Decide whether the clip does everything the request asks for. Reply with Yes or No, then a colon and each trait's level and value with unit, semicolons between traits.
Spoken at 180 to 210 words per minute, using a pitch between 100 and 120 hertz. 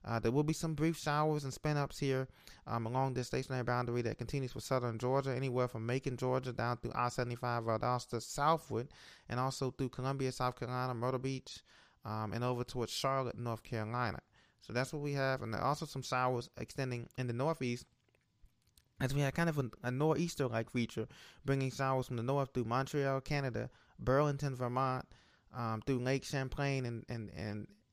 No: average, 190 wpm; low, 130 Hz